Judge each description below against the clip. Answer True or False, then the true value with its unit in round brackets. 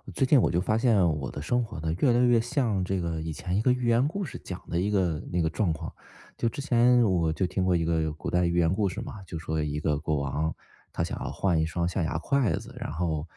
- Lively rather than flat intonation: True (6.1 semitones)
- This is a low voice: True (90 Hz)